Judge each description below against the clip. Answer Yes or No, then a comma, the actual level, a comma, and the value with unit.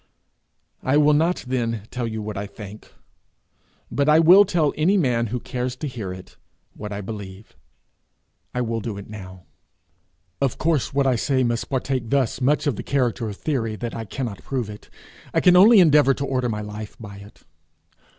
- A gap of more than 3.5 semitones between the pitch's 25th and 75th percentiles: Yes, average, 4.8 semitones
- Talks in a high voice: No, low, 125 Hz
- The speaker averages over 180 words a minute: Yes, average, 190 wpm